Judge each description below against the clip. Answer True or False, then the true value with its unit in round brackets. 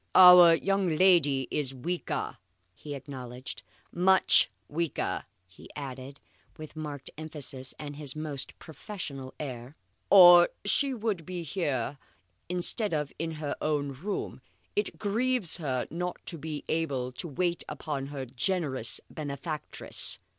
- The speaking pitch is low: False (155 Hz)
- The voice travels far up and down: False (4.4 semitones)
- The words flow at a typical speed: False (125 wpm)